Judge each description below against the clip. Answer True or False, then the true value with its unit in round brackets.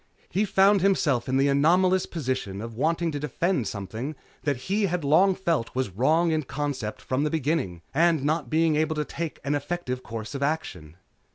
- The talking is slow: False (185 wpm)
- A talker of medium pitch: True (150 Hz)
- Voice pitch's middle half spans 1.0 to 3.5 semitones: False (4.7 semitones)